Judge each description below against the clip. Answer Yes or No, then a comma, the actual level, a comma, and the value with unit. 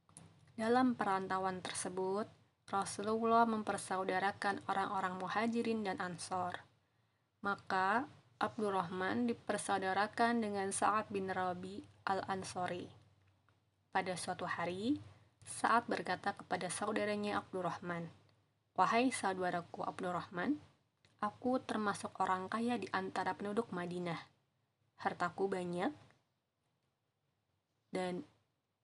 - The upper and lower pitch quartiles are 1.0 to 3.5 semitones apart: Yes, average, 2.8 semitones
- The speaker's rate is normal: No, slow, 80 wpm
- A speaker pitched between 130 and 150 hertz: No, high, 190 Hz